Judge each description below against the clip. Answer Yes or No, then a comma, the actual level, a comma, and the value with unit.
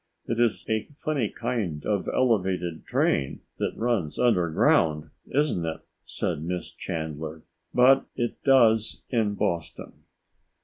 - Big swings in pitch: Yes, wide, 6.7 semitones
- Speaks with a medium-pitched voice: No, low, 105 Hz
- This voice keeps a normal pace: No, slow, 120 wpm